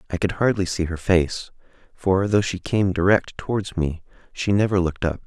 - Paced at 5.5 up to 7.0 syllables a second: No, 5.1 syllables/s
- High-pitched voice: No, very low, 95 Hz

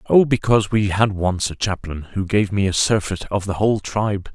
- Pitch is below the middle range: Yes, low, 100 Hz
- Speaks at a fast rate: Yes, fast, 220 wpm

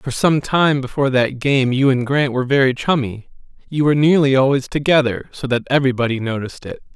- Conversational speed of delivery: Yes, average, 190 wpm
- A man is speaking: Yes, male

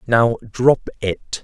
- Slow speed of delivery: Yes, slow, 125 wpm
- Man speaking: Yes, male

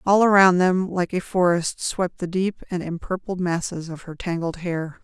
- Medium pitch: Yes, medium, 180 Hz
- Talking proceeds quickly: No, average, 190 wpm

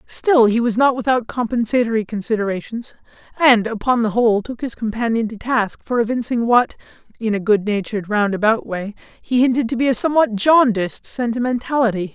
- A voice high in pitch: Yes, high, 230 Hz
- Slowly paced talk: No, average, 165 wpm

